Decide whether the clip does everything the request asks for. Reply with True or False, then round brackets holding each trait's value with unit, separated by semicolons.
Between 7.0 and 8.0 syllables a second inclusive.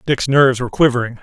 True (7.2 syllables/s)